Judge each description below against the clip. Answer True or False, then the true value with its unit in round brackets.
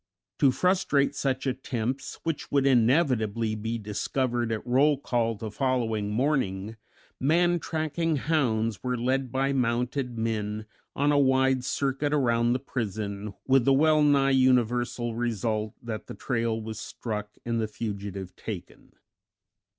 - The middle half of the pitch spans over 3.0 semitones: True (3.6 semitones)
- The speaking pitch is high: False (125 Hz)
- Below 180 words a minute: True (135 wpm)